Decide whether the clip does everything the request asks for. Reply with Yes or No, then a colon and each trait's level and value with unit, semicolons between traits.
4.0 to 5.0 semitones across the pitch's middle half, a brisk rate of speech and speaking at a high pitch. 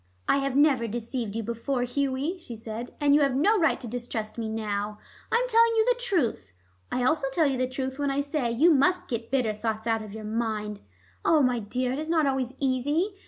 Yes: average, 4.4 semitones; fast, 225 wpm; very high, 255 Hz